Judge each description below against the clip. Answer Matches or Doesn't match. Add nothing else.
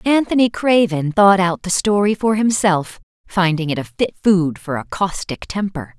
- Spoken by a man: Doesn't match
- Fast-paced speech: Doesn't match